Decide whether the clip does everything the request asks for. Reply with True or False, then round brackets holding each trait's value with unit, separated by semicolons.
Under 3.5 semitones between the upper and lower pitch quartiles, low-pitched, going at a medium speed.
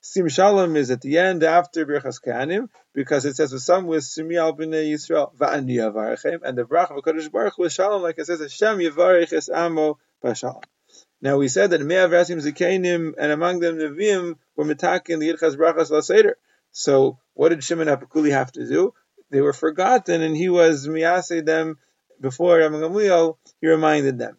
False (2.9 semitones; 160 Hz; 170 wpm)